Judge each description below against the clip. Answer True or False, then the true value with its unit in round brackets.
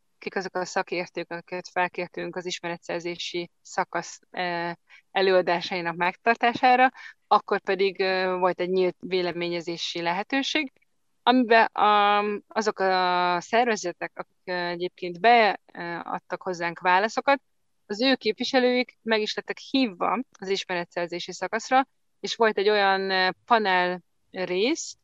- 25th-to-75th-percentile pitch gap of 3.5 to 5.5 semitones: True (3.8 semitones)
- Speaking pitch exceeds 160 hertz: True (190 Hz)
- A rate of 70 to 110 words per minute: True (105 wpm)